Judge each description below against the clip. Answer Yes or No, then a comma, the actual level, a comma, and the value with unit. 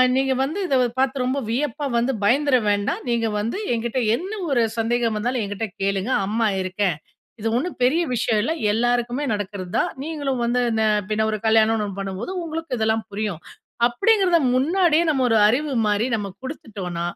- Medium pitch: No, high, 235 Hz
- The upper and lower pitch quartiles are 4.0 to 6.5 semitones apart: Yes, average, 4.4 semitones